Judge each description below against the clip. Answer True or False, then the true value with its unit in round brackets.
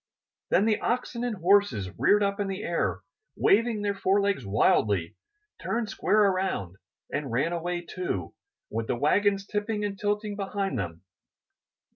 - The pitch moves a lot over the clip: True (6.3 semitones)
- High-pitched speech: True (195 Hz)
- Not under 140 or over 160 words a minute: True (145 wpm)